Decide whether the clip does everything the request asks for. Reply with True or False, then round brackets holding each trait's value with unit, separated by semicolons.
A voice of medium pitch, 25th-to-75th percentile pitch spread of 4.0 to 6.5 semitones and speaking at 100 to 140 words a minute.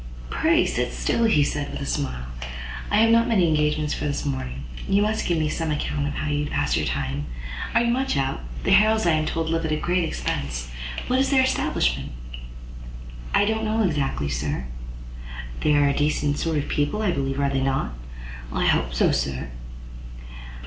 False (150 Hz; 5.2 semitones; 190 wpm)